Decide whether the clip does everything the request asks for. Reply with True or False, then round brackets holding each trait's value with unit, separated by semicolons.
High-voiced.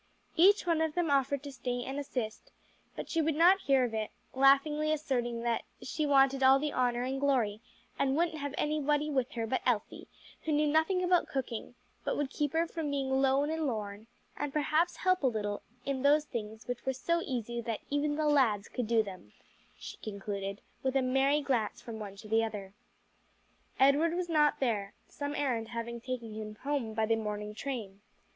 True (265 Hz)